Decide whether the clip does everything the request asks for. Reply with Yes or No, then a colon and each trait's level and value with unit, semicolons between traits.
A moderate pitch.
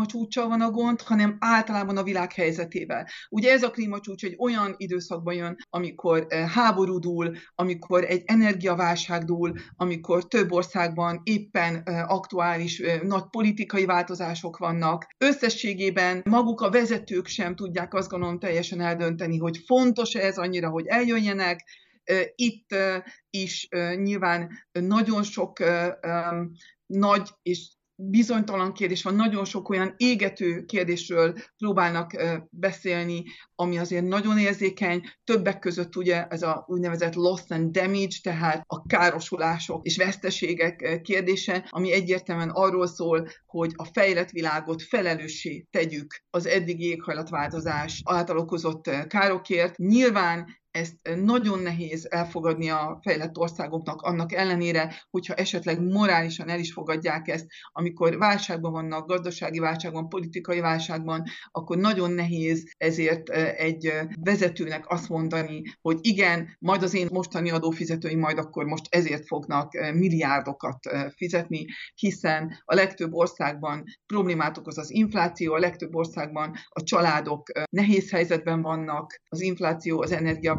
Yes: medium, 175 Hz